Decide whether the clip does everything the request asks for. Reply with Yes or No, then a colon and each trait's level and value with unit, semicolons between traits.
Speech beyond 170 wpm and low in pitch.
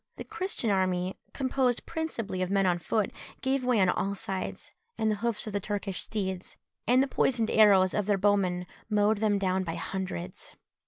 No: average, 180 wpm; high, 205 Hz